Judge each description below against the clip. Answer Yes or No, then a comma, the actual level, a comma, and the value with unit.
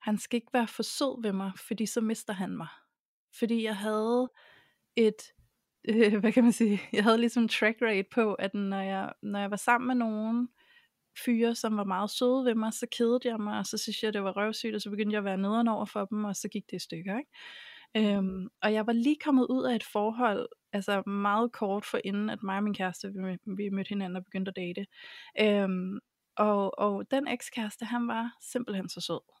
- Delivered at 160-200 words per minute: No, average, 220 wpm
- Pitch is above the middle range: Yes, high, 215 Hz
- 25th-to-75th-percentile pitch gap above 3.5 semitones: No, average, 2.8 semitones